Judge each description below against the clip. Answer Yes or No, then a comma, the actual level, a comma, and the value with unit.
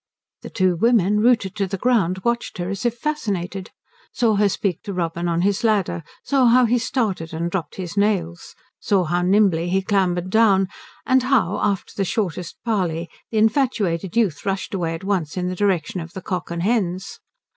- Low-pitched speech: No, high, 195 Hz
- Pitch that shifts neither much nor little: Yes, average, 3.7 semitones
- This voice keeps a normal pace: Yes, average, 190 wpm